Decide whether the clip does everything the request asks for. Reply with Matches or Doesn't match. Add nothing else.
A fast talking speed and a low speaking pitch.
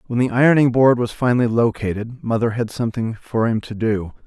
Doesn't match